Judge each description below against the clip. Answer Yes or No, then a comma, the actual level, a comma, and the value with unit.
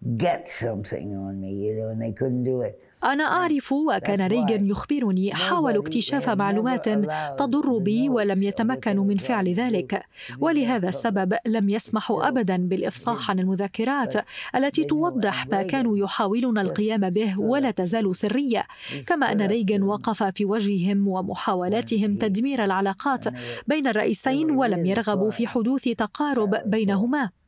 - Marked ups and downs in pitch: No, average, 3.9 semitones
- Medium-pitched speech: No, high, 215 Hz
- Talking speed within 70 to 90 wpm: No, average, 110 wpm